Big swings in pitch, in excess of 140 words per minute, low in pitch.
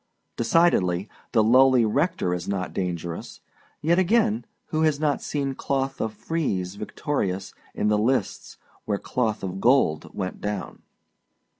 No: wide, 7.2 semitones; slow, 135 wpm; low, 115 Hz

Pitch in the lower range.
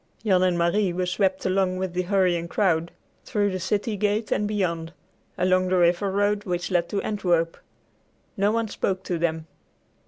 No: medium, 185 Hz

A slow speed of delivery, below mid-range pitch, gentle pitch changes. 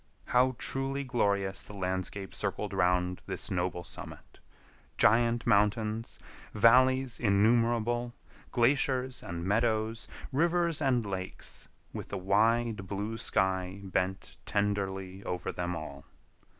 No: slow, 105 wpm; low, 105 Hz; average, 4.0 semitones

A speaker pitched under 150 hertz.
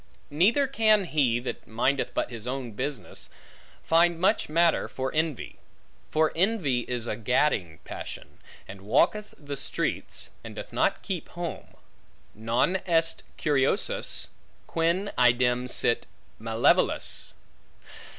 Yes: medium, 140 Hz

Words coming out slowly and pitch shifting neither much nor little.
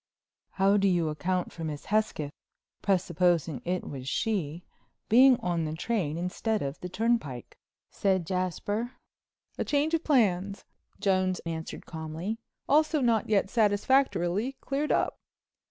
Yes: slow, 120 wpm; average, 4.9 semitones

